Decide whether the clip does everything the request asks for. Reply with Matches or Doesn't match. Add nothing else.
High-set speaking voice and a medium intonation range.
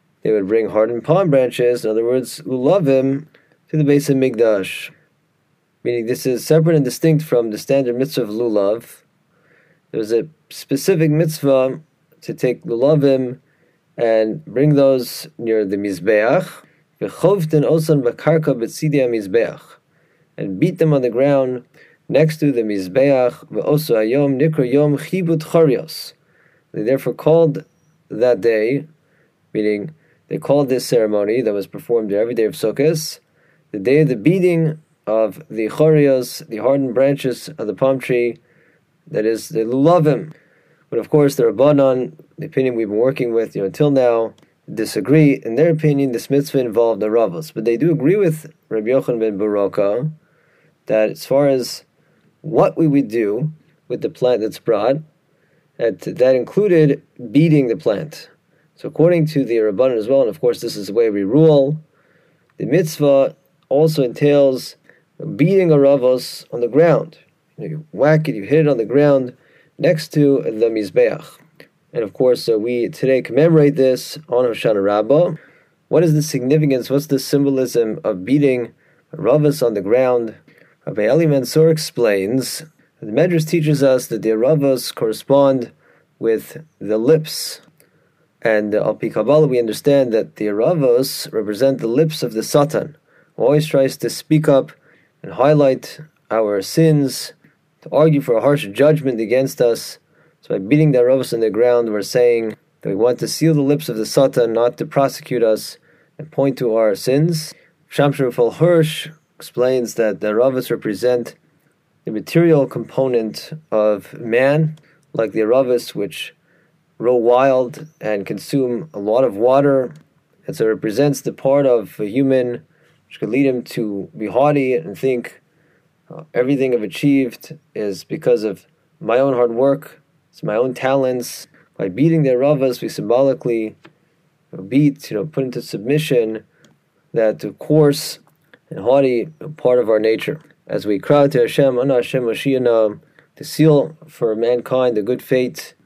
Doesn't match